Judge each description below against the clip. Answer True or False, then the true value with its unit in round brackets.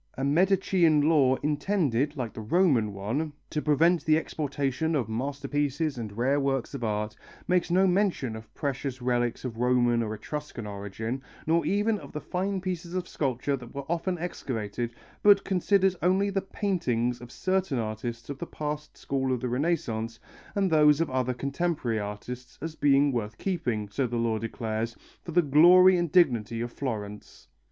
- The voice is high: False (140 Hz)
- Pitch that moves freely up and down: True (6.2 semitones)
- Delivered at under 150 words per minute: False (170 wpm)